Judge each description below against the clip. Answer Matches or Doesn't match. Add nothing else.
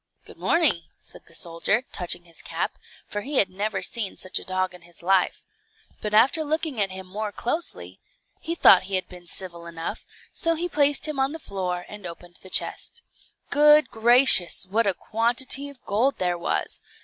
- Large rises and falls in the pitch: Matches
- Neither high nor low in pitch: Doesn't match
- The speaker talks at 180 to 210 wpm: Matches